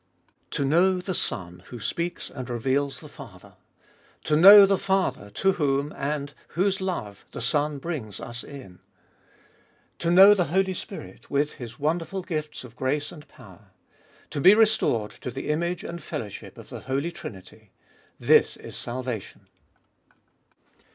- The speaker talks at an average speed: Yes, average, 150 wpm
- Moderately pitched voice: Yes, medium, 145 Hz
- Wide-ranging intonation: Yes, wide, 6.1 semitones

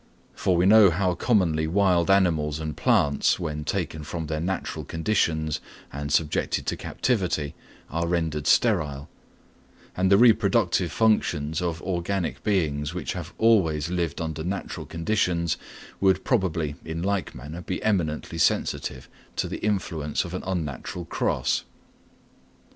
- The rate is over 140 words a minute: No, slow, 135 wpm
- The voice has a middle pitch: No, very low, 85 Hz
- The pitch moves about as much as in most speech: Yes, average, 3.6 semitones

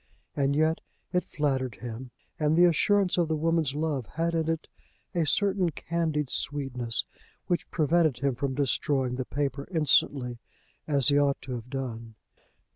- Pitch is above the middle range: No, medium, 145 Hz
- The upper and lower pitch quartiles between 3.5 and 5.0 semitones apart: Yes, average, 3.8 semitones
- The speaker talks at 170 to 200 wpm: No, average, 155 wpm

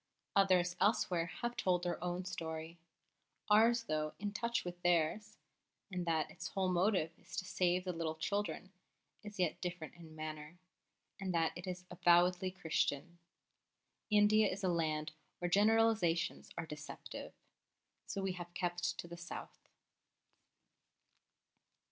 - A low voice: No, medium, 175 Hz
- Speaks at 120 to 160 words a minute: Yes, slow, 135 wpm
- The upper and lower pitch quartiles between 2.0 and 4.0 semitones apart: Yes, average, 2.7 semitones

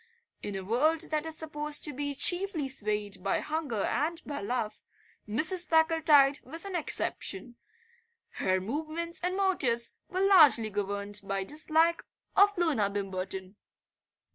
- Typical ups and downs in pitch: No, wide, 7.8 semitones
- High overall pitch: Yes, very high, 290 Hz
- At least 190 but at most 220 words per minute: No, slow, 135 wpm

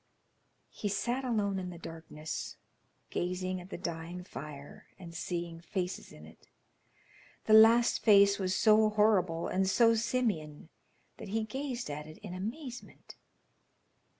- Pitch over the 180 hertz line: Yes, high, 190 Hz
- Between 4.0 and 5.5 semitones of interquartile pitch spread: Yes, average, 4.4 semitones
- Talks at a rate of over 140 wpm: No, slow, 135 wpm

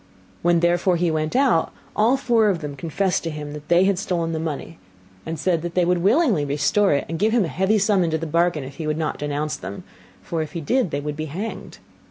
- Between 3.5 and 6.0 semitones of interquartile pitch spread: Yes, average, 3.9 semitones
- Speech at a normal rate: No, fast, 245 wpm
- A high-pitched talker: No, medium, 170 Hz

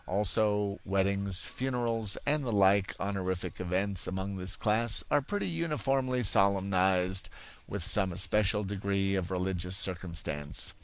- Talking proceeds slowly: Yes, slow, 120 wpm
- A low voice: Yes, low, 100 Hz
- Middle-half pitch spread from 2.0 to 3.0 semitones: Yes, narrow, 2.4 semitones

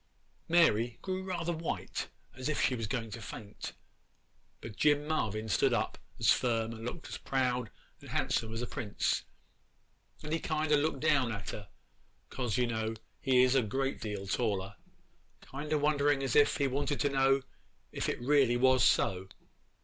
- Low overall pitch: Yes, low, 130 Hz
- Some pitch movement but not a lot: Yes, average, 4.5 semitones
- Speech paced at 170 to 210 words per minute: Yes, average, 180 wpm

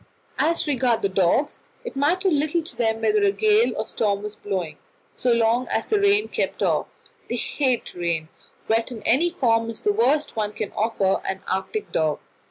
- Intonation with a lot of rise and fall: Yes, wide, 8.5 semitones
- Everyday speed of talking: Yes, average, 180 wpm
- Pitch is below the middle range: No, high, 235 Hz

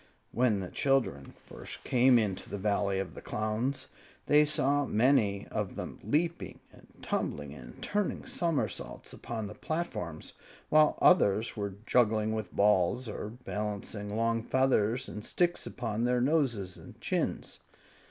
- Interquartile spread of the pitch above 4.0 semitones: Yes, average, 4.5 semitones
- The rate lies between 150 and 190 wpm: No, average, 140 wpm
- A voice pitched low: Yes, low, 110 Hz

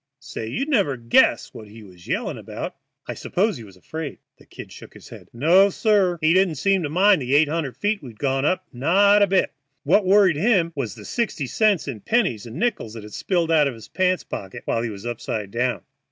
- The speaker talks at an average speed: No, fast, 220 wpm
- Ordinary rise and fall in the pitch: No, wide, 8.4 semitones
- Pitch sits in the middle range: Yes, medium, 155 Hz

